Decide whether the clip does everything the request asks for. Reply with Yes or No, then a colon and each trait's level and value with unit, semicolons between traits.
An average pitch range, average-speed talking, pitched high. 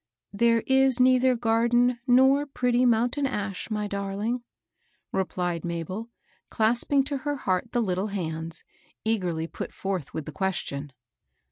No: average, 5.0 semitones; slow, 130 wpm; high, 225 Hz